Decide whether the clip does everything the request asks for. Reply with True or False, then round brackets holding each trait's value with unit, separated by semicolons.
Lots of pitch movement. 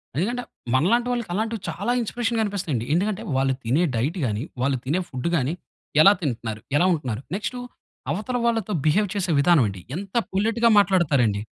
True (8.4 semitones)